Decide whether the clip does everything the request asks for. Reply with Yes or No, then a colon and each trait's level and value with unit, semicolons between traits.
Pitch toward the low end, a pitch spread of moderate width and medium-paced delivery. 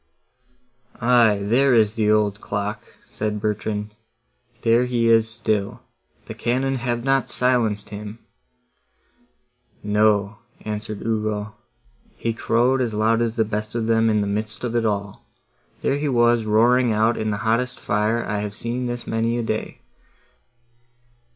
No: low, 110 Hz; narrow, 2.0 semitones; average, 145 wpm